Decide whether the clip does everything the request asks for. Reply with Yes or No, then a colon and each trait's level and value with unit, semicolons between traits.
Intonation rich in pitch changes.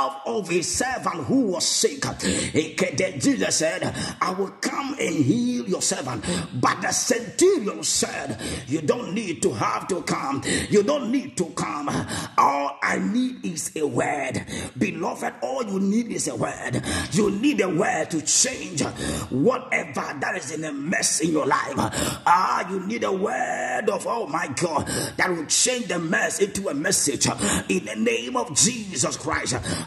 Yes: wide, 6.5 semitones